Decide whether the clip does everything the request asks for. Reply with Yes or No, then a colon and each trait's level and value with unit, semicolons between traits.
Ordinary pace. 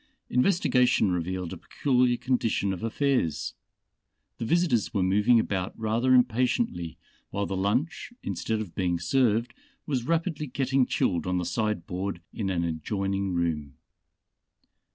No: slow, 130 wpm